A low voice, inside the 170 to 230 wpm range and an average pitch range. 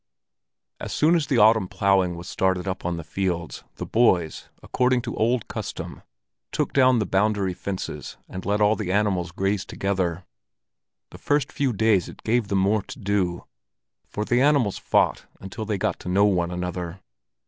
Yes: low, 100 Hz; average, 175 wpm; average, 3.5 semitones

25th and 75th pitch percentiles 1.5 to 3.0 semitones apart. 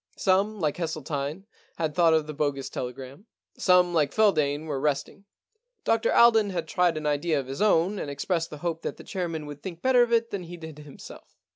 No: average, 4.4 semitones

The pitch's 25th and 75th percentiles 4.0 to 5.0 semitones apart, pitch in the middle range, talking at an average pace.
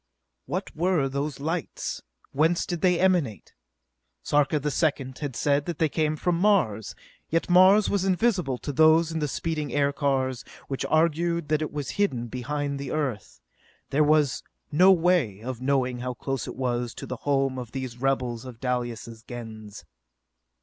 Yes: average, 4.3 semitones; medium, 145 Hz; average, 165 wpm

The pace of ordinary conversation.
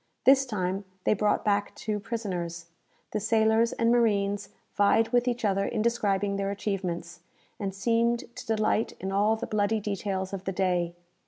Yes: average, 165 wpm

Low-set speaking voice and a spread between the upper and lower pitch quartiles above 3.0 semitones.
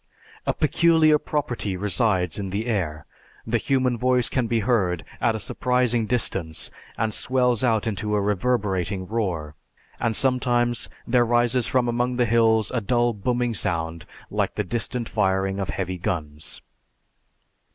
Yes: low, 115 Hz; average, 4.1 semitones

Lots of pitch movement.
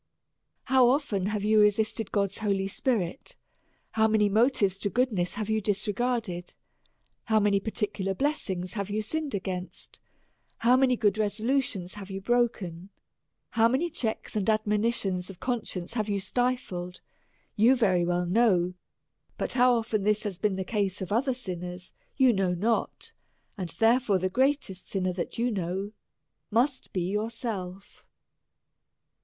No: average, 3.8 semitones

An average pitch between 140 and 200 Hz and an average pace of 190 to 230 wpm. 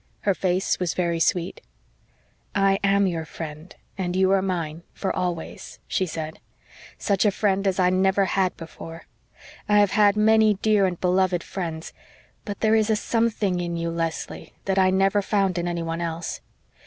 No: medium, 185 Hz; average, 170 wpm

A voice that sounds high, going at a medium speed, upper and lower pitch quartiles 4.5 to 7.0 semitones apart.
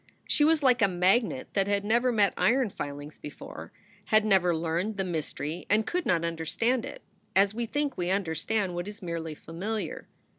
Yes: high, 200 Hz; average, 180 wpm; average, 5.3 semitones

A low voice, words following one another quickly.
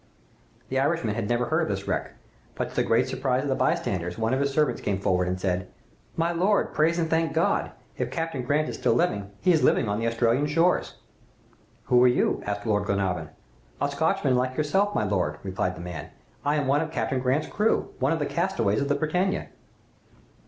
Yes: low, 130 Hz; fast, 210 wpm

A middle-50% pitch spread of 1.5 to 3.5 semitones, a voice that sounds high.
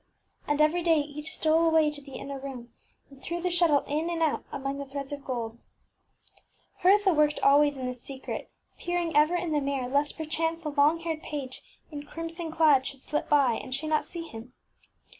Yes: average, 2.9 semitones; very high, 295 Hz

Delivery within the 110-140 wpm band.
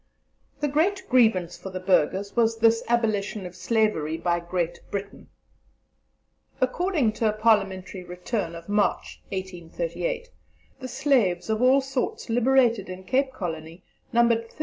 Yes: slow, 135 wpm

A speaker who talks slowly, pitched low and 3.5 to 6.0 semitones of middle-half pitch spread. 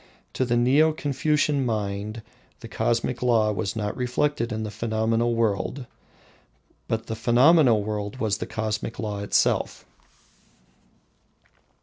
No: slow, 120 wpm; low, 115 Hz; average, 2.8 semitones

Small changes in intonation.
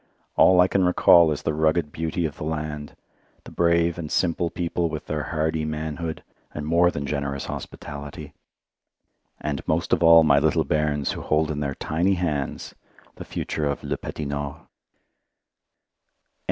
Yes: narrow, 2.2 semitones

